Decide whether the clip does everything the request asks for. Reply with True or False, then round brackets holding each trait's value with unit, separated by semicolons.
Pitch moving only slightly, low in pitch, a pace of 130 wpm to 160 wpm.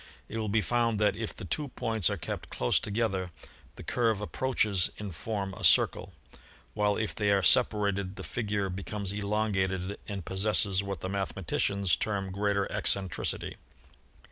True (1.9 semitones; 100 Hz; 155 wpm)